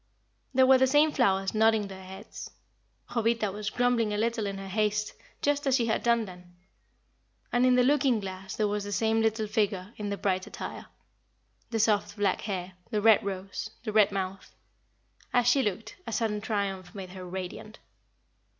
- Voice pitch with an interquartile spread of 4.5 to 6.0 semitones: No, average, 3.1 semitones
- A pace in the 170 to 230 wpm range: Yes, average, 180 wpm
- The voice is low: No, high, 210 Hz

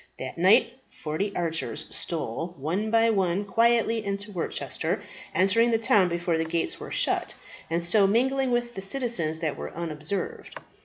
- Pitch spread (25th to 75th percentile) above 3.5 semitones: Yes, wide, 5.4 semitones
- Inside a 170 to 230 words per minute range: No, average, 160 wpm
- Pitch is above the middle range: Yes, high, 195 Hz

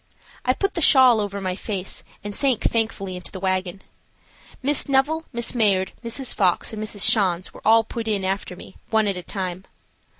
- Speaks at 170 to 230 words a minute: Yes, average, 190 wpm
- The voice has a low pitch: No, high, 210 Hz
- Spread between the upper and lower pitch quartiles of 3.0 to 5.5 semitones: Yes, average, 4.0 semitones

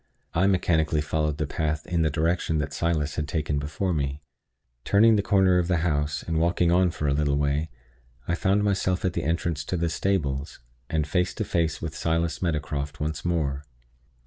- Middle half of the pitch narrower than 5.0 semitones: Yes, average, 2.9 semitones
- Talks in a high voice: No, very low, 80 Hz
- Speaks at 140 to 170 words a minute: No, average, 190 wpm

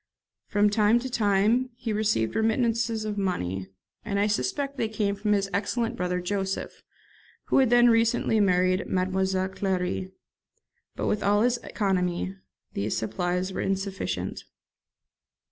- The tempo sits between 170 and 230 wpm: No, slow, 135 wpm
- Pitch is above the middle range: Yes, high, 205 Hz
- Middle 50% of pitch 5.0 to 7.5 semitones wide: No, average, 3.1 semitones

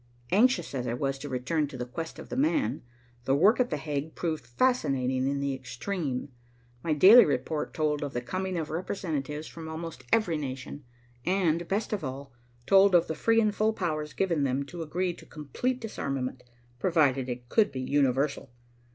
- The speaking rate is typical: Yes, average, 185 wpm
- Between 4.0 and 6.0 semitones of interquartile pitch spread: Yes, wide, 5.4 semitones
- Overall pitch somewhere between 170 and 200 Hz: No, medium, 155 Hz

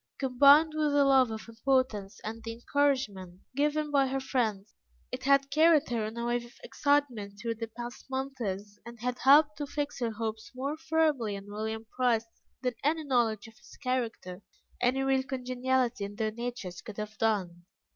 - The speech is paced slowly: No, average, 175 wpm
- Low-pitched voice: No, high, 245 Hz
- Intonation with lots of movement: No, average, 3.9 semitones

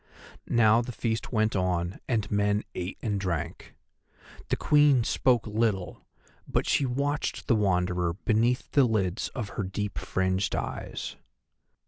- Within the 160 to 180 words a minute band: No, slow, 135 wpm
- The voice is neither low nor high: No, low, 105 Hz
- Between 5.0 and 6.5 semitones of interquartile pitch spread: No, average, 4.2 semitones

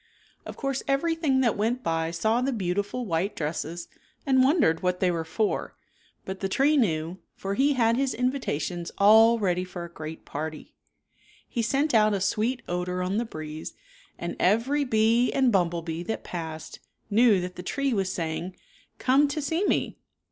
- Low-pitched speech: No, high, 205 Hz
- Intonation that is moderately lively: No, wide, 6.5 semitones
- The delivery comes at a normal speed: Yes, average, 180 wpm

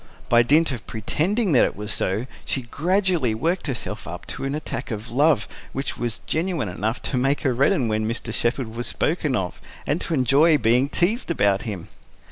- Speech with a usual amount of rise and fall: No, wide, 5.7 semitones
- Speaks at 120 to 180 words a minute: No, average, 190 wpm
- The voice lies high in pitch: No, low, 130 Hz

